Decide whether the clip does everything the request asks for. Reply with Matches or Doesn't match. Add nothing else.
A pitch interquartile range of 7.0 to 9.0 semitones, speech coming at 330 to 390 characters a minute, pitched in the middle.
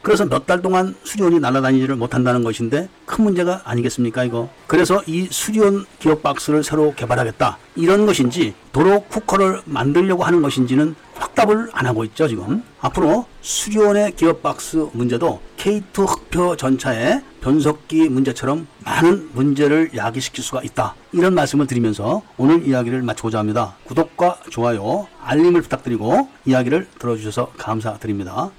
Doesn't match